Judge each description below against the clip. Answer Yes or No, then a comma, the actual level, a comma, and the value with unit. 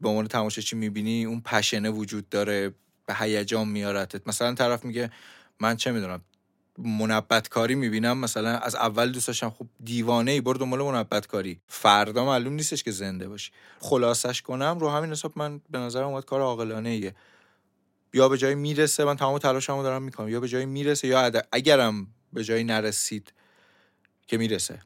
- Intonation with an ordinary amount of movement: Yes, average, 3.3 semitones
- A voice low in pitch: Yes, low, 115 Hz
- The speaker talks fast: Yes, fast, 170 wpm